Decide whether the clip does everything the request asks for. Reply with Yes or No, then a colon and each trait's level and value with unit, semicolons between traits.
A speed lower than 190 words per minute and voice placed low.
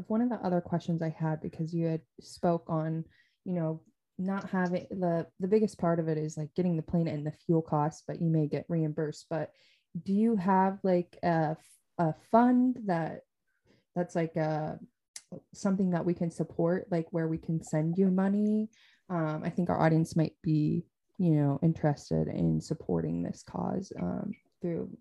No: average, 180 wpm; medium, 165 Hz